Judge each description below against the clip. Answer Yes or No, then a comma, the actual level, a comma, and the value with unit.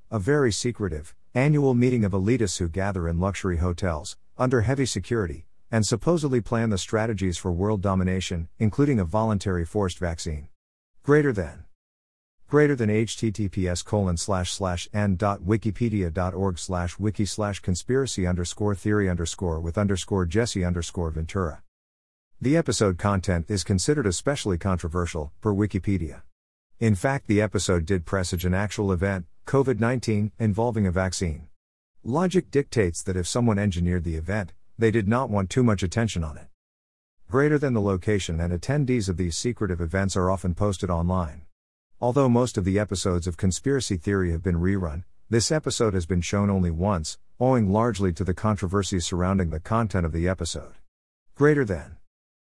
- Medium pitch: No, very low, 95 Hz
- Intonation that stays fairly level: No, average, 3.9 semitones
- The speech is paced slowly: No, average, 150 wpm